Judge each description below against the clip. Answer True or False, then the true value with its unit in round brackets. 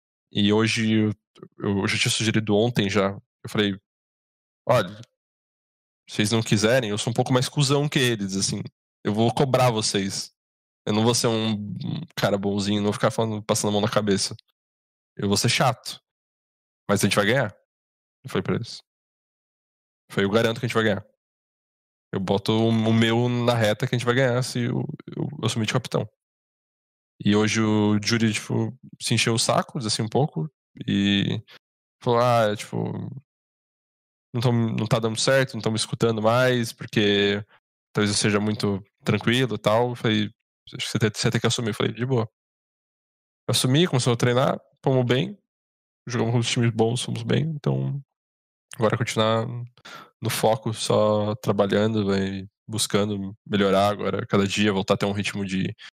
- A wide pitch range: False (3.0 semitones)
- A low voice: True (110 Hz)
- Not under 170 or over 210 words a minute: True (175 wpm)